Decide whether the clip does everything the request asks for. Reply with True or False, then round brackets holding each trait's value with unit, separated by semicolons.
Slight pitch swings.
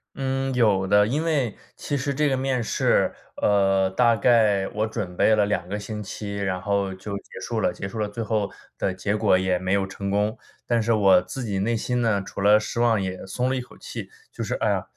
False (3.4 semitones)